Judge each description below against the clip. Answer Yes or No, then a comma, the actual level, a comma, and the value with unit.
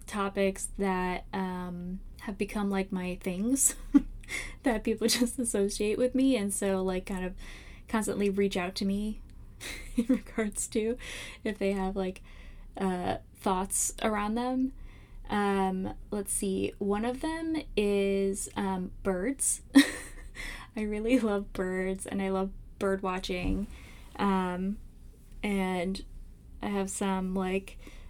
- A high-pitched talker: Yes, high, 200 Hz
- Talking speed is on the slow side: Yes, slow, 125 wpm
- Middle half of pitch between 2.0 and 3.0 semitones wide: Yes, average, 2.7 semitones